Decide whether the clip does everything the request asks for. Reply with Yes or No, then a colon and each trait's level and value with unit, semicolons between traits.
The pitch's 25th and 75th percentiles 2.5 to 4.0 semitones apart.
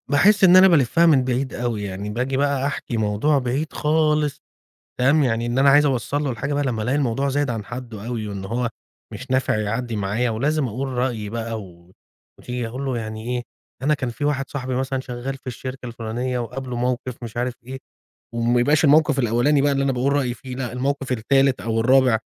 Yes: average, 2.9 semitones